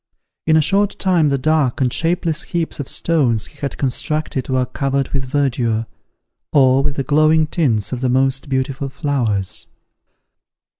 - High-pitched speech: No, medium, 140 Hz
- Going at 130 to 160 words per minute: Yes, average, 155 wpm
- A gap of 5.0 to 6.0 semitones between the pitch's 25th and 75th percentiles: No, average, 3.1 semitones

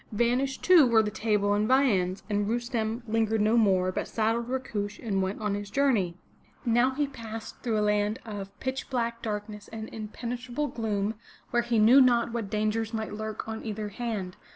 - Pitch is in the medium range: No, high, 220 Hz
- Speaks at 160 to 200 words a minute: Yes, average, 180 wpm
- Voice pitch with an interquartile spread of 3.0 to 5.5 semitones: No, narrow, 2.4 semitones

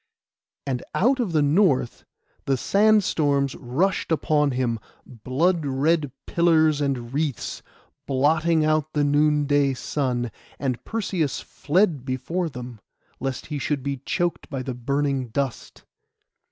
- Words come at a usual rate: No, slow, 125 wpm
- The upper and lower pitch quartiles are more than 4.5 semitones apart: No, average, 3.5 semitones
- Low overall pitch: No, medium, 145 Hz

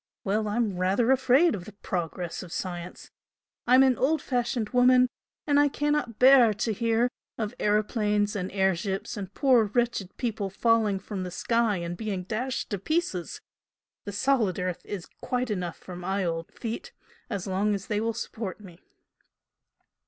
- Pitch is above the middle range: Yes, high, 210 Hz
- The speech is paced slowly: No, average, 165 wpm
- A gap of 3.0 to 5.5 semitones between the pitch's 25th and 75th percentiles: Yes, average, 4.4 semitones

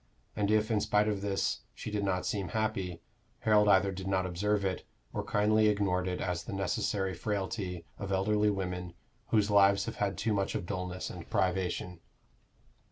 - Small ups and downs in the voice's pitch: Yes, narrow, 2.2 semitones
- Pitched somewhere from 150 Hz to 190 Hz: No, low, 100 Hz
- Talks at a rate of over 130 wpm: Yes, average, 175 wpm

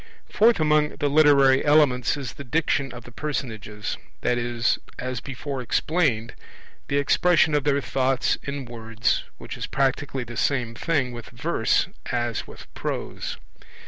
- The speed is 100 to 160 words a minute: Yes, average, 145 wpm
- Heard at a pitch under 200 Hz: Yes, low, 135 Hz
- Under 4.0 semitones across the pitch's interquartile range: Yes, average, 3.5 semitones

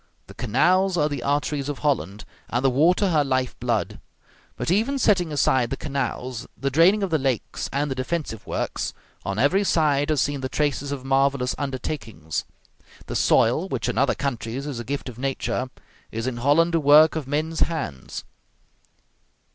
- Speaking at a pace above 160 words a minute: Yes, average, 175 wpm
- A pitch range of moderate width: Yes, average, 3.5 semitones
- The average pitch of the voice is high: No, medium, 140 Hz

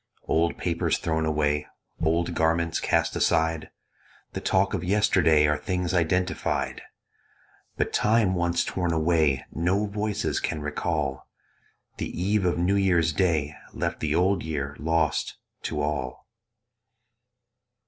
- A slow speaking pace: Yes, slow, 125 wpm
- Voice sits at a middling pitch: No, very low, 85 Hz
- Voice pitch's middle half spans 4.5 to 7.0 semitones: No, average, 3.0 semitones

